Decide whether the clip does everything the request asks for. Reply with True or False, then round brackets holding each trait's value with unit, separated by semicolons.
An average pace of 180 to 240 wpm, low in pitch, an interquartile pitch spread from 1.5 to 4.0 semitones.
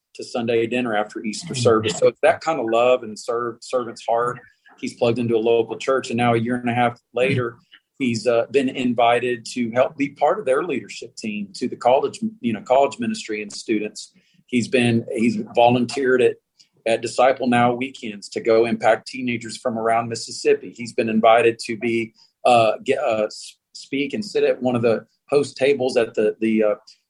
True (195 wpm; 120 Hz; 3.4 semitones)